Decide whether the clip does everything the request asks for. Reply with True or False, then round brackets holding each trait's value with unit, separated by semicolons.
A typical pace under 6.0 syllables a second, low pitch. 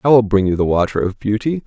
False (6.4 syllables/s; 110 Hz)